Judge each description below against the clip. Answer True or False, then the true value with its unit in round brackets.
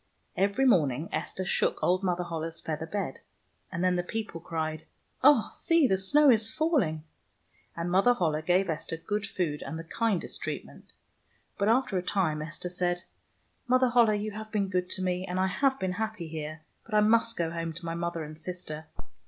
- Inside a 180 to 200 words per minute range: True (195 wpm)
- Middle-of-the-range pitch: True (180 Hz)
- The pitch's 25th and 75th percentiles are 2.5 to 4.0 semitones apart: False (4.6 semitones)